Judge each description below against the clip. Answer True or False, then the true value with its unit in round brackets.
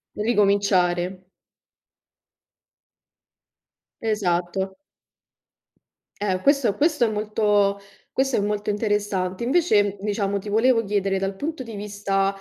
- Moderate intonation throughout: False (2.1 semitones)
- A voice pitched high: True (205 Hz)